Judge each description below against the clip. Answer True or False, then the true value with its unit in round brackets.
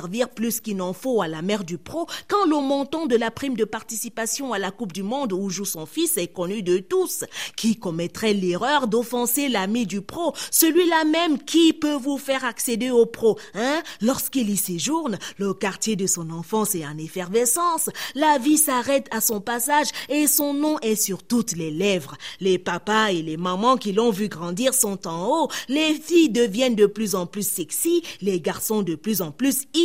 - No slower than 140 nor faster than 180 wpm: False (195 wpm)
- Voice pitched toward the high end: True (225 Hz)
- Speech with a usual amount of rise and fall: False (6.3 semitones)